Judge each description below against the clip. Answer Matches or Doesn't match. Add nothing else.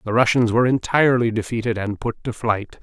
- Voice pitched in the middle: Doesn't match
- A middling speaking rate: Matches